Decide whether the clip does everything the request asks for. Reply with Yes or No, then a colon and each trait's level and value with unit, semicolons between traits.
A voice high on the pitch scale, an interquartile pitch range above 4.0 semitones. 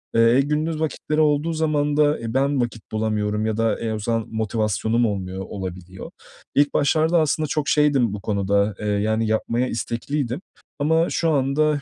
No: low, 120 Hz; wide, 5.6 semitones